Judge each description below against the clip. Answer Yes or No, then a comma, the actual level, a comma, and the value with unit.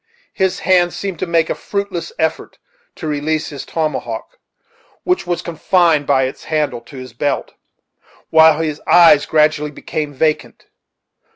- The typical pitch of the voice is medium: Yes, medium, 155 Hz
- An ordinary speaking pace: Yes, average, 145 wpm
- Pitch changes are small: No, average, 3.0 semitones